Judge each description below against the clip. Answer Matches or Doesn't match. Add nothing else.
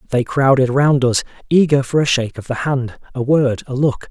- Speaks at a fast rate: Matches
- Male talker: Matches